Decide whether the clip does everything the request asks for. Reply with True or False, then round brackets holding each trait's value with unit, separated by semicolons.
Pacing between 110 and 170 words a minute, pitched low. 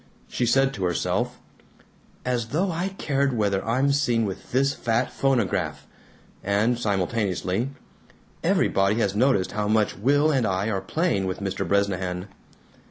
True (140 wpm; 110 Hz)